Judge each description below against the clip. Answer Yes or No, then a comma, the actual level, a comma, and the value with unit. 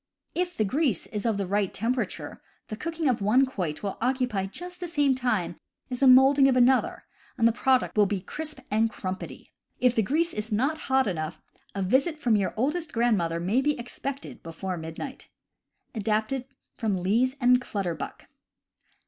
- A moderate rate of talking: Yes, average, 175 wpm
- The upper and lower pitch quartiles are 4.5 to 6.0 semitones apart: Yes, average, 5.1 semitones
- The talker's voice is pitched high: Yes, high, 240 Hz